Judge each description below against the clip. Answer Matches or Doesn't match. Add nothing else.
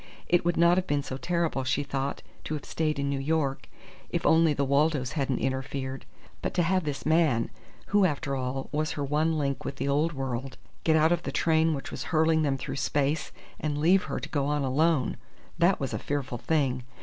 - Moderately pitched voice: Matches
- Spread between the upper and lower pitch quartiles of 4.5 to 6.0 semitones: Doesn't match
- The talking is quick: Matches